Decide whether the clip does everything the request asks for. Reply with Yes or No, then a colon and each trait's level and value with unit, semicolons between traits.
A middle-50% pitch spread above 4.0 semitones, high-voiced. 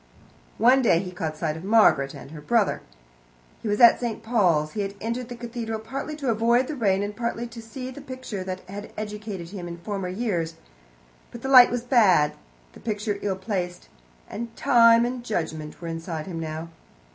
Yes: average, 5.0 semitones; high, 210 Hz